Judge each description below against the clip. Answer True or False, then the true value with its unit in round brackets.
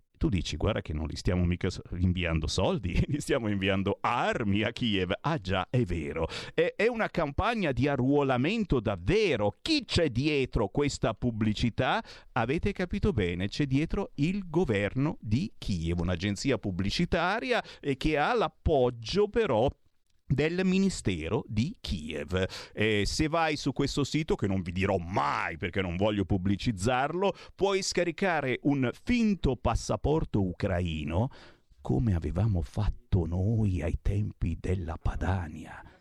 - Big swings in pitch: True (7.6 semitones)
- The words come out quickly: False (130 wpm)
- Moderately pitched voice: False (110 Hz)